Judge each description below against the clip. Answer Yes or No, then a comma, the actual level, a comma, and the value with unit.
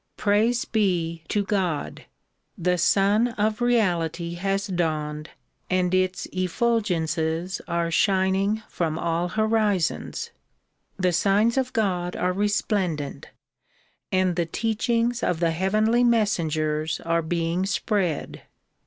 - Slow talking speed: Yes, slow, 110 wpm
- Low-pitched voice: No, medium, 185 Hz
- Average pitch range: Yes, average, 4.0 semitones